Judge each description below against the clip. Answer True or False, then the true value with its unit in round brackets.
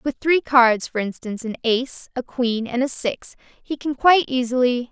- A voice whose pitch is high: True (250 Hz)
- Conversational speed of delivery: True (195 wpm)